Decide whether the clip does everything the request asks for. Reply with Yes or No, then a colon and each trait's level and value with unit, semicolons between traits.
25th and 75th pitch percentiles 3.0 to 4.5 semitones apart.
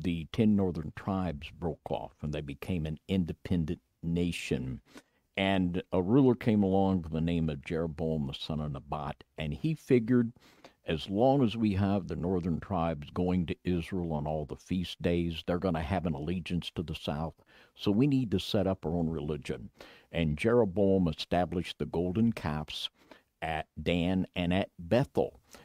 Yes: average, 3.3 semitones